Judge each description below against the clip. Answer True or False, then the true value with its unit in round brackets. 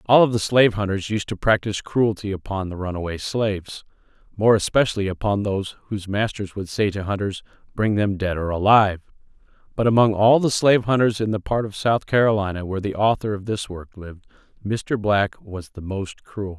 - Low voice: True (105 Hz)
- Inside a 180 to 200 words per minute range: True (190 wpm)